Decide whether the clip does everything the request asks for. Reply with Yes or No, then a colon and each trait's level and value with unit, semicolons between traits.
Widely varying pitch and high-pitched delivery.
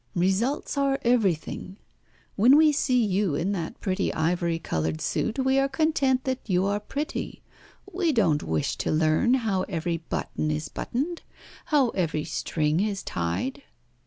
Yes: wide, 8.2 semitones; high, 200 Hz